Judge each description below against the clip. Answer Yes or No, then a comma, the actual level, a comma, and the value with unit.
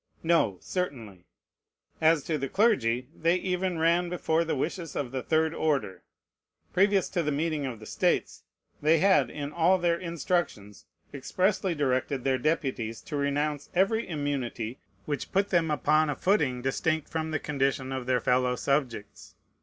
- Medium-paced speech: Yes, average, 155 wpm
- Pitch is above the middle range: No, medium, 150 Hz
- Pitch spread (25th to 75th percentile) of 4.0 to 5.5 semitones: Yes, average, 4.4 semitones